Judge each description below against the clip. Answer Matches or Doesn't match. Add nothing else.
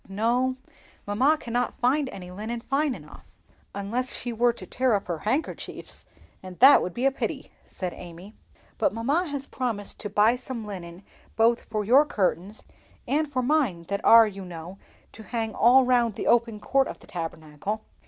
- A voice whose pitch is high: Matches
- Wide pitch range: Doesn't match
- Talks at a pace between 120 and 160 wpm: Doesn't match